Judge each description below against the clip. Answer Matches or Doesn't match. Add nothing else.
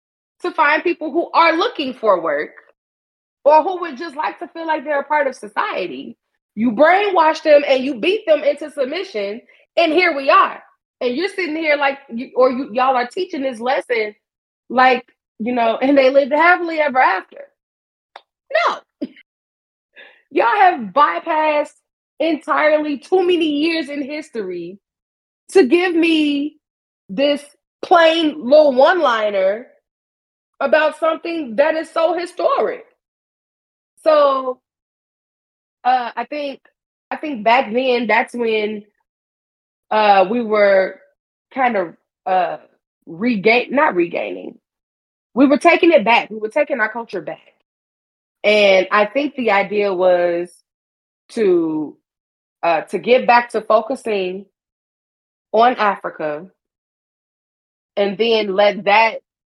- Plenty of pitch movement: Matches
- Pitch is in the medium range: Doesn't match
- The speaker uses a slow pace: Matches